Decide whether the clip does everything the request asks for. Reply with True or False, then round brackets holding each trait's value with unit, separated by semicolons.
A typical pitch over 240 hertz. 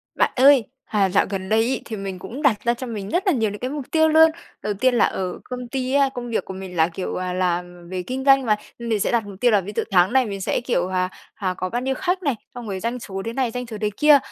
False (225 Hz)